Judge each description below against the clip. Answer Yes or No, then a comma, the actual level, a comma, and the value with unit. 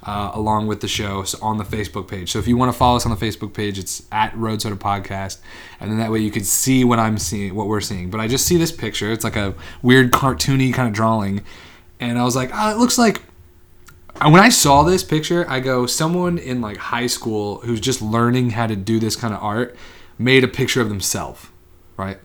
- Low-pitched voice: Yes, low, 110 Hz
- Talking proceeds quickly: Yes, fast, 245 wpm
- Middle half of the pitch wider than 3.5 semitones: Yes, average, 4.0 semitones